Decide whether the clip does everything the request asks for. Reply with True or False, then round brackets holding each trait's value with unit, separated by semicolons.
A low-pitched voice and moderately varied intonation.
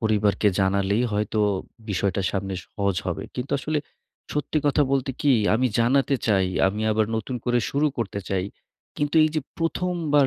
False (115 Hz; 5.9 semitones)